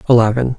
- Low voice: Yes, low, 120 Hz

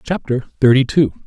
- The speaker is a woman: No, male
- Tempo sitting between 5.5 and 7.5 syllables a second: No, 5.3 syllables/s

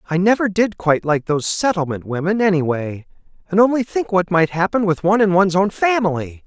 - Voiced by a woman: No, male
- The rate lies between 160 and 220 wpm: Yes, average, 195 wpm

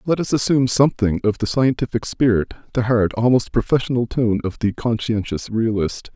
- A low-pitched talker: Yes, low, 115 Hz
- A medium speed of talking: Yes, average, 165 wpm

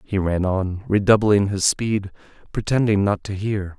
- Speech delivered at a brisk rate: No, average, 160 wpm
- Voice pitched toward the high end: No, low, 100 Hz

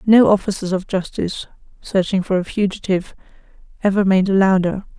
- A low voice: No, high, 190 Hz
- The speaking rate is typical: Yes, average, 145 wpm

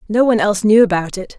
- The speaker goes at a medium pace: No, fast, 260 wpm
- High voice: Yes, high, 205 Hz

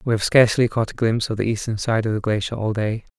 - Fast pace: Yes, fast, 285 wpm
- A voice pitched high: No, low, 110 Hz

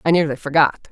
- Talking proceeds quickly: No, average, 195 wpm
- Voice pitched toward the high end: No, medium, 145 Hz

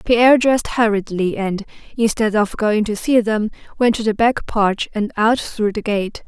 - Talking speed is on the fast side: No, average, 190 wpm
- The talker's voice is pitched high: Yes, high, 220 Hz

